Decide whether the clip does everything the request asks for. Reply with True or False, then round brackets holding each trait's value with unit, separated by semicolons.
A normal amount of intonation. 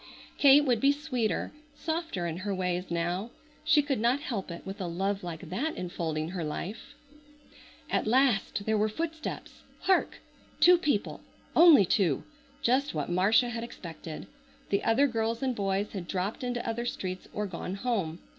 False (6.0 semitones)